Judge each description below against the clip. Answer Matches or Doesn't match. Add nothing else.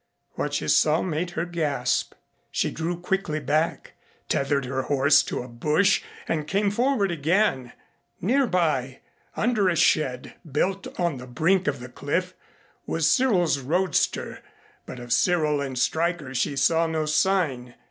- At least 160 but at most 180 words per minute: Doesn't match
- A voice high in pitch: Doesn't match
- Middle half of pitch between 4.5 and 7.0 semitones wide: Matches